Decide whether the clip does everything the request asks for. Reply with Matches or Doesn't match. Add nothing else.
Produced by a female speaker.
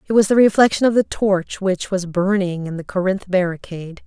Matches